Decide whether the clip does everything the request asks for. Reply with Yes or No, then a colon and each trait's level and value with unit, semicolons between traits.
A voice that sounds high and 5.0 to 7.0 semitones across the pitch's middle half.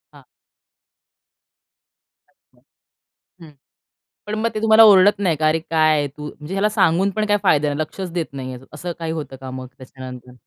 No: medium, 160 Hz; wide, 5.4 semitones